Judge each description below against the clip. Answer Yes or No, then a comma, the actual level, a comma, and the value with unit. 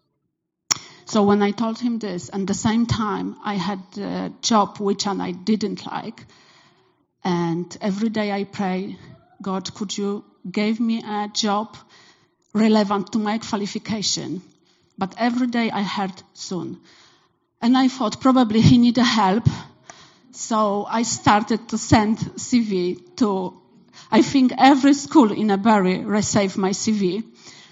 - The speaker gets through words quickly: No, slow, 135 wpm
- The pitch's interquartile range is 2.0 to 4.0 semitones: Yes, narrow, 2.6 semitones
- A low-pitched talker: No, high, 210 Hz